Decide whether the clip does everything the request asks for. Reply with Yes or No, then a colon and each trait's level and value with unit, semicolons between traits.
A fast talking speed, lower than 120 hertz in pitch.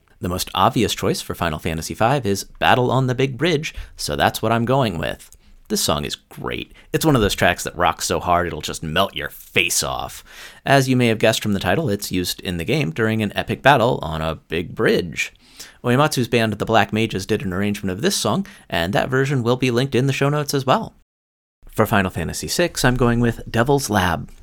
Yes: fast, 225 wpm; low, 110 Hz